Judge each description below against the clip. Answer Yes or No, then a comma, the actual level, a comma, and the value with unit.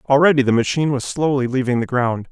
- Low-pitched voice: Yes, low, 130 Hz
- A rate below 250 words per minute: Yes, fast, 205 wpm